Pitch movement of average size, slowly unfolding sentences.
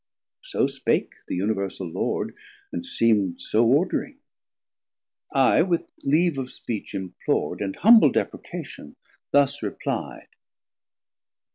No: wide, 7.0 semitones; slow, 105 wpm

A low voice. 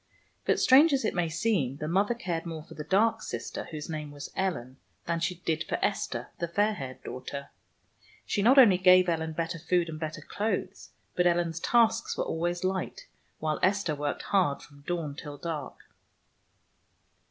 No: medium, 170 Hz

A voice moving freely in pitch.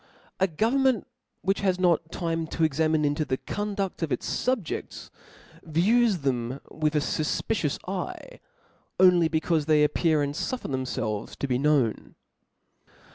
No: average, 4.4 semitones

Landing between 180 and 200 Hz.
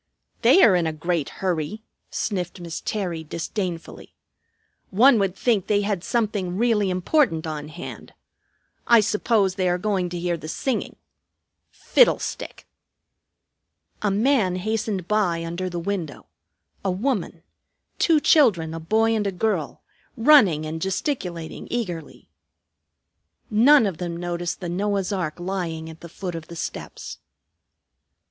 Yes: medium, 185 Hz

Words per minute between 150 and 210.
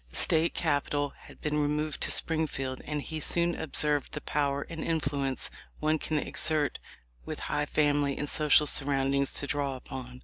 Yes: average, 165 wpm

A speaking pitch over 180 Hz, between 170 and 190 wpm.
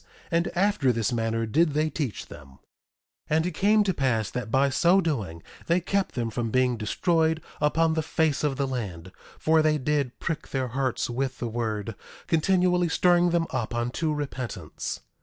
No: medium, 140 Hz; average, 175 wpm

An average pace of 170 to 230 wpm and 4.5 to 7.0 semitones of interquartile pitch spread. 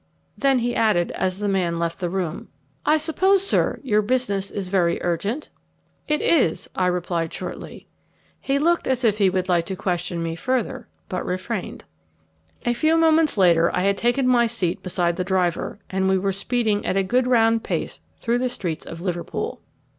Yes: average, 185 wpm; wide, 5.5 semitones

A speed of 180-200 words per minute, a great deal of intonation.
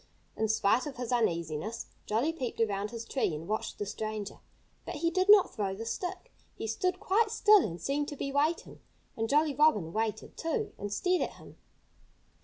Yes: average, 190 wpm; wide, 7.8 semitones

